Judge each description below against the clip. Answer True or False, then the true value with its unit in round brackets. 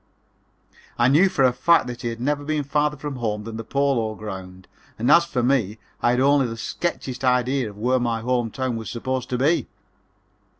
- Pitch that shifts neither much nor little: True (3.5 semitones)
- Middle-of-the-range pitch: False (125 Hz)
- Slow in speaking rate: False (205 wpm)